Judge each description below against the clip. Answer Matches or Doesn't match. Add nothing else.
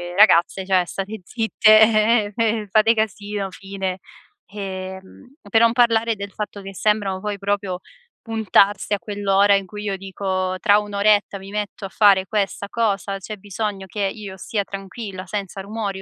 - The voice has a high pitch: Matches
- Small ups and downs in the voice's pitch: Matches